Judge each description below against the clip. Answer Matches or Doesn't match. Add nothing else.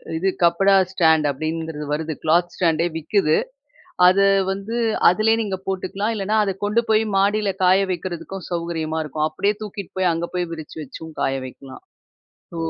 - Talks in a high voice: Doesn't match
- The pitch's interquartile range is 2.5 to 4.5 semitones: Matches